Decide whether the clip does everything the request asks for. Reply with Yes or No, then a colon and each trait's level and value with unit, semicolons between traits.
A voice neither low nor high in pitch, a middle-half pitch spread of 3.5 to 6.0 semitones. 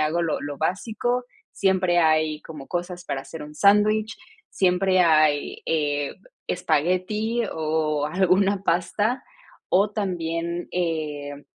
Yes: medium, 175 Hz; average, 3.8 semitones